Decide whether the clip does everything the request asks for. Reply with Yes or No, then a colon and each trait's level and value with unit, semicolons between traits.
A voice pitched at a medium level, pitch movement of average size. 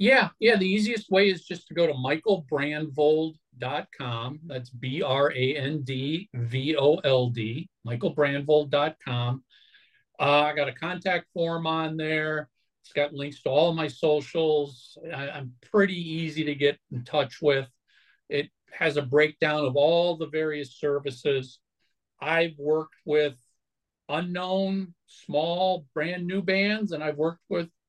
Yes: medium, 150 Hz; average, 3.3 semitones